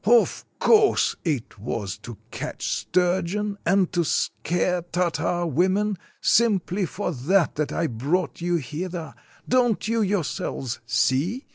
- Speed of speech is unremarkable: No, slow, 125 wpm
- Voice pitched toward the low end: No, medium, 180 Hz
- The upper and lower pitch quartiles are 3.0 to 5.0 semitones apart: Yes, average, 4.3 semitones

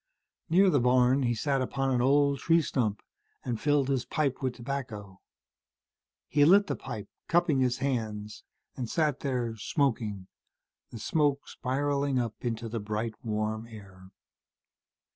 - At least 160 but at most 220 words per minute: No, average, 145 wpm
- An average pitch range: Yes, average, 4.1 semitones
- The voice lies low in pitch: Yes, low, 125 Hz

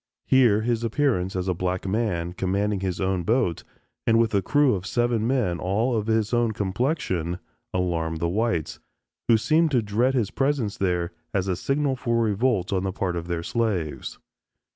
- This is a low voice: Yes, low, 105 Hz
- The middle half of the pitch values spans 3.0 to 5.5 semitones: Yes, average, 4.6 semitones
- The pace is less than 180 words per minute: No, average, 185 wpm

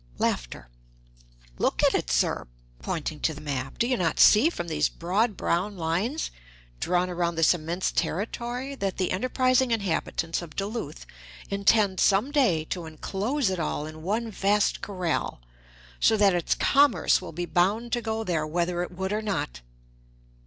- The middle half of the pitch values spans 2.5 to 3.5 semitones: No, average, 4.9 semitones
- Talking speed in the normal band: Yes, average, 160 wpm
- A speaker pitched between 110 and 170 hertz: No, medium, 185 Hz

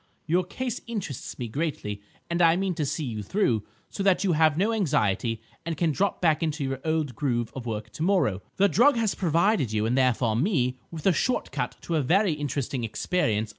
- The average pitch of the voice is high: No, medium, 155 Hz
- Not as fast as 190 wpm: No, average, 200 wpm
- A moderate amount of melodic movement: No, wide, 7.0 semitones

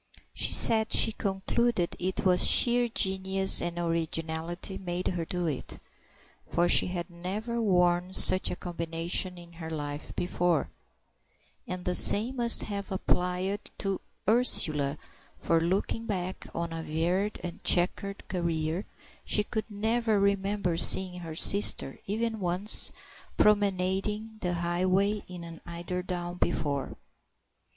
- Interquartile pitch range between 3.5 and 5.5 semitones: No, average, 2.8 semitones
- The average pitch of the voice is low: No, medium, 180 Hz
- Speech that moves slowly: Yes, slow, 130 wpm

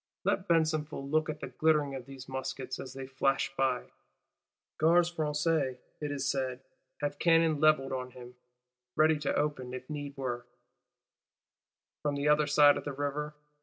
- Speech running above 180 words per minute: No, average, 160 wpm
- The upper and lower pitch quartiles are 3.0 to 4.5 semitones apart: No, narrow, 2.5 semitones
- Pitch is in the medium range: Yes, medium, 145 Hz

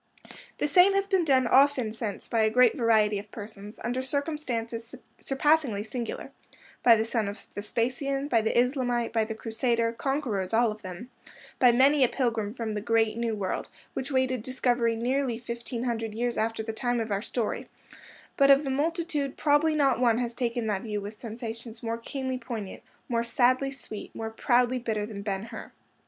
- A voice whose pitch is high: Yes, high, 235 Hz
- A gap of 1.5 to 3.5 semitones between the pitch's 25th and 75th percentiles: Yes, average, 2.8 semitones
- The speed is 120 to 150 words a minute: No, average, 180 wpm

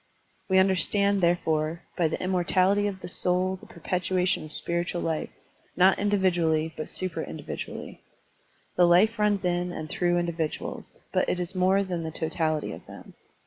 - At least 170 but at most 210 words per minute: No, average, 155 wpm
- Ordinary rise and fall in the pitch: No, narrow, 2.1 semitones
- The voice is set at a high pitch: No, medium, 180 Hz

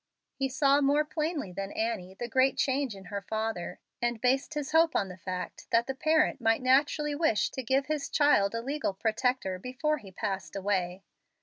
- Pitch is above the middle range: Yes, very high, 250 Hz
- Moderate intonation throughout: No, wide, 6.3 semitones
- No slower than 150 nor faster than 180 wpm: No, average, 190 wpm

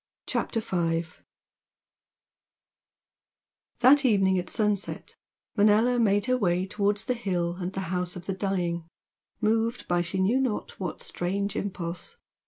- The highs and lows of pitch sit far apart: No, average, 3.6 semitones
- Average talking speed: No, slow, 130 wpm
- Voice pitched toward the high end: Yes, high, 195 Hz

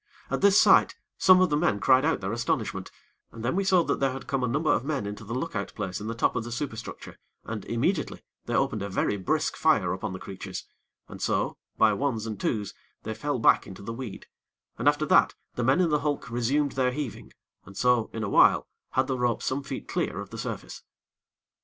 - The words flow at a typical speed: No, fast, 225 wpm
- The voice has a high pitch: No, low, 125 Hz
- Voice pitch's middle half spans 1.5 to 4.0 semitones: No, average, 4.9 semitones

